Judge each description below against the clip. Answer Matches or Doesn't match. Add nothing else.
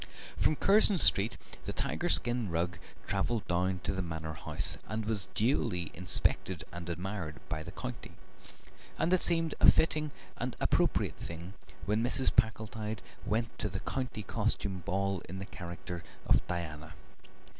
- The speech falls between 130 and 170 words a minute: Matches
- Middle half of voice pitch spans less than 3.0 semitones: Doesn't match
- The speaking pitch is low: Matches